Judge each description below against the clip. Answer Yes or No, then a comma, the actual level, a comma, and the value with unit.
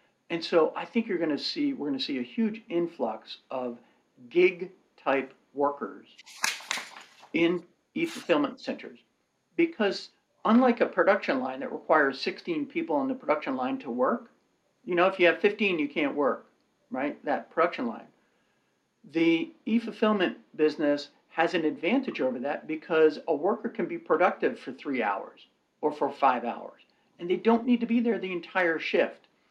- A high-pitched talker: Yes, high, 215 Hz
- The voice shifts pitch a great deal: Yes, wide, 8.3 semitones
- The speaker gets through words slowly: No, average, 170 wpm